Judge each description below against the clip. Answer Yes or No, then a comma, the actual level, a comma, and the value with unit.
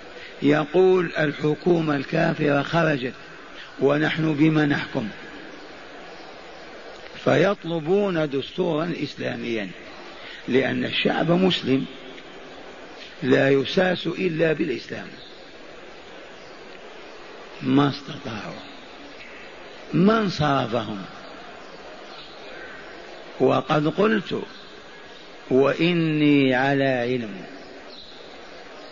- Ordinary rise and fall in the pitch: Yes, average, 3.6 semitones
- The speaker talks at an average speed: No, slow, 55 wpm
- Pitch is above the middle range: No, medium, 155 Hz